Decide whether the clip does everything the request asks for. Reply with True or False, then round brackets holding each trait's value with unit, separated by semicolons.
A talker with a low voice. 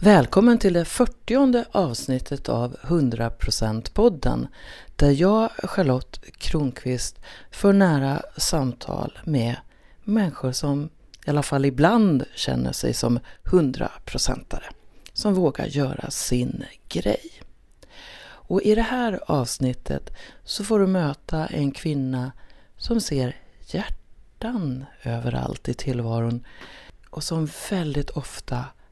False (145 Hz)